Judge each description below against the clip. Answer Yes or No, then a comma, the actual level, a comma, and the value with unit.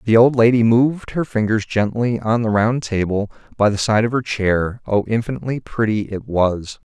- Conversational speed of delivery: Yes, average, 190 wpm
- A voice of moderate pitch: No, low, 110 Hz